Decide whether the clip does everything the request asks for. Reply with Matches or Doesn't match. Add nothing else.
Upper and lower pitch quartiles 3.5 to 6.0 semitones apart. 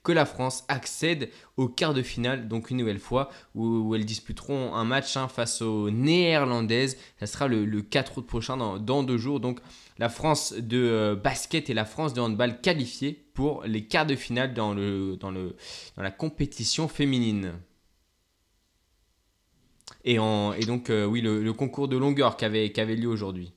Matches